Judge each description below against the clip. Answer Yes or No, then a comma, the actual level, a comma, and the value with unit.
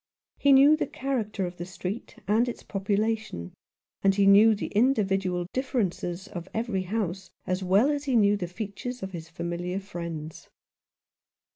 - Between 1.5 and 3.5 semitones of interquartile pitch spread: No, average, 3.9 semitones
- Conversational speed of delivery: Yes, average, 155 wpm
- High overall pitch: Yes, high, 200 Hz